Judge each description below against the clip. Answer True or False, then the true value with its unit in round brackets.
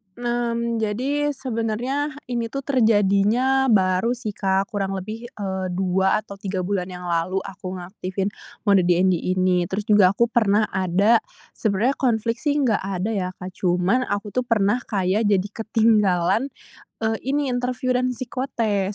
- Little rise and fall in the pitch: False (4.0 semitones)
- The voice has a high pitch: True (210 Hz)